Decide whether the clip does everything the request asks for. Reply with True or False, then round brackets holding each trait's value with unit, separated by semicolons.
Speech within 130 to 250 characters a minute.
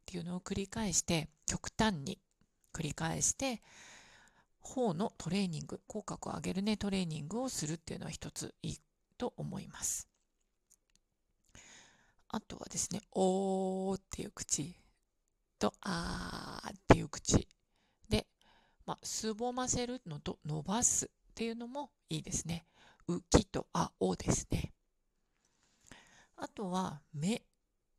True (240 characters per minute)